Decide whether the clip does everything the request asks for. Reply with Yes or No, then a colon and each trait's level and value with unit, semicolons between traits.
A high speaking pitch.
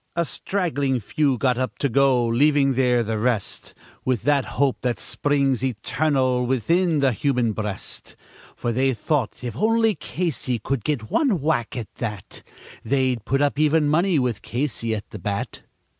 No: low, 130 Hz